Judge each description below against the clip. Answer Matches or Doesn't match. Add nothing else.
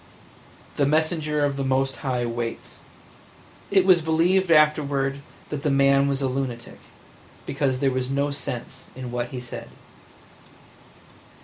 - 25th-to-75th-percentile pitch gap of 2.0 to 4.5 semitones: Matches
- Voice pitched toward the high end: Doesn't match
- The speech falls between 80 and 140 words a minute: Matches